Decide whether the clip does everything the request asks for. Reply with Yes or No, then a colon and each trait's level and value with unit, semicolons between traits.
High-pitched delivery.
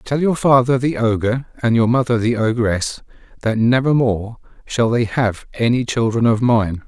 No: low, 120 Hz